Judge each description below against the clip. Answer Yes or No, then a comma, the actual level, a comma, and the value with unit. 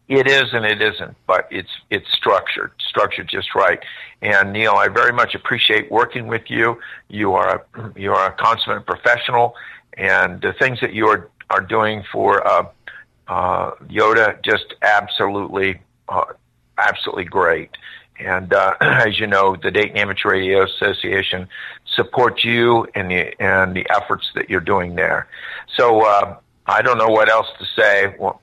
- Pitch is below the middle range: Yes, low, 105 Hz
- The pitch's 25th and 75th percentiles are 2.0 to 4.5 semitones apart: Yes, average, 3.5 semitones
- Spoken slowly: No, average, 165 wpm